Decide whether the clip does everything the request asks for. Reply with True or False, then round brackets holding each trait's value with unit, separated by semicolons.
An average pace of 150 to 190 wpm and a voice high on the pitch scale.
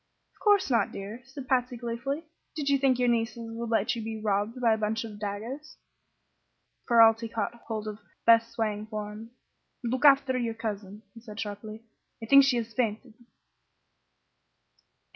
True (160 wpm; 230 Hz)